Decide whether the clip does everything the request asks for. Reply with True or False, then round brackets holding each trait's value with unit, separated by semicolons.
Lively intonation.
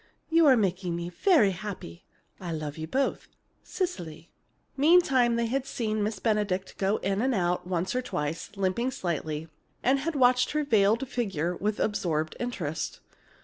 True (6.3 semitones)